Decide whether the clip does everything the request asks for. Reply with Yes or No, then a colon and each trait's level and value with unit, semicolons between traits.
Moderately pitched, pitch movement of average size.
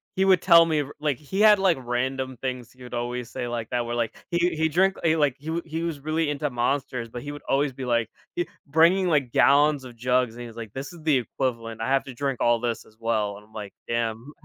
No: low, 130 Hz; average, 4.7 semitones